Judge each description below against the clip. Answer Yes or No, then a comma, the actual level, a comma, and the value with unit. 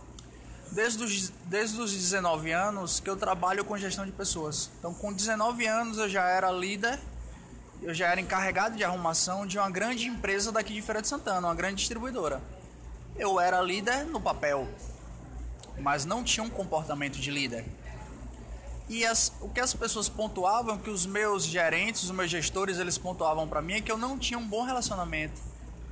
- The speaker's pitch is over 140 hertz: Yes, medium, 185 Hz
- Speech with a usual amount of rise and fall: No, wide, 6.4 semitones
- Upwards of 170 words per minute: Yes, average, 180 wpm